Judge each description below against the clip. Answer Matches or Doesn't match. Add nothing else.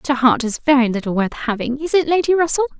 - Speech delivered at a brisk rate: Matches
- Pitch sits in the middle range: Doesn't match